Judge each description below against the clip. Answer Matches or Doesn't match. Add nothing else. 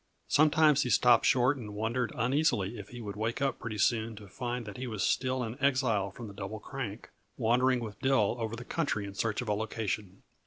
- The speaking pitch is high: Doesn't match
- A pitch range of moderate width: Matches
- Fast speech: Matches